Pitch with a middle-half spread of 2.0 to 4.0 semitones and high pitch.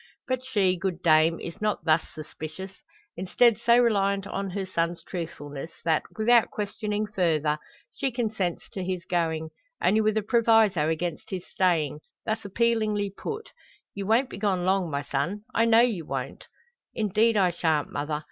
No: average, 4.6 semitones; high, 195 Hz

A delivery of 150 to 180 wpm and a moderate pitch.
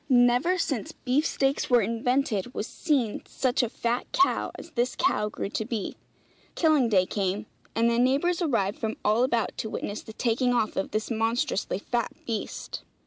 No: average, 175 wpm; high, 235 Hz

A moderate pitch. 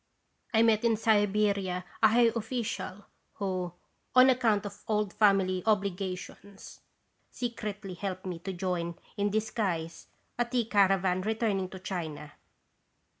No: high, 200 Hz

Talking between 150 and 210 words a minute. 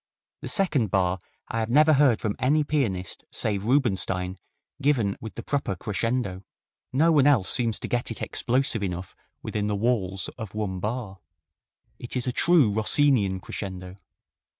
Yes: average, 160 wpm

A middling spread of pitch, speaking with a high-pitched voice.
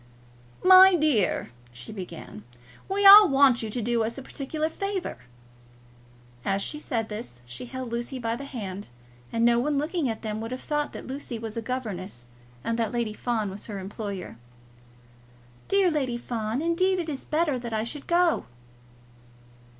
No: wide, 5.7 semitones; high, 240 Hz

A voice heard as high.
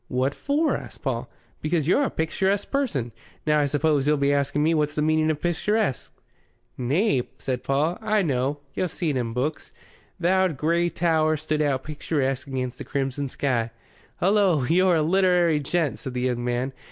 No: medium, 150 Hz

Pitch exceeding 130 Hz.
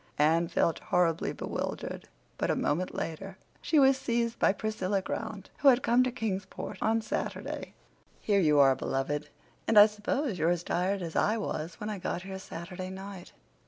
Yes: high, 190 Hz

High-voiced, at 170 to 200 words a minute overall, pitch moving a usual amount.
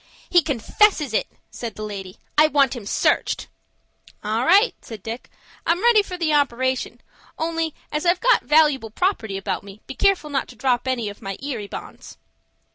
No: very high, 270 Hz; average, 175 wpm; wide, 6.8 semitones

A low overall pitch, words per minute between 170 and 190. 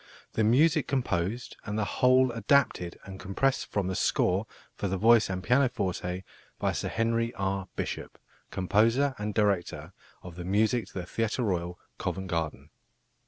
No: low, 105 Hz; average, 155 wpm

